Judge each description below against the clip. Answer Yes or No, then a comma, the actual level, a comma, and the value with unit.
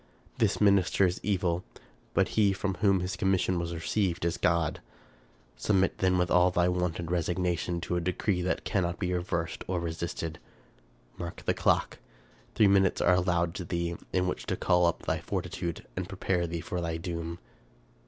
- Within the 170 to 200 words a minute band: Yes, average, 175 wpm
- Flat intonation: Yes, narrow, 1.6 semitones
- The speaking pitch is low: Yes, very low, 90 Hz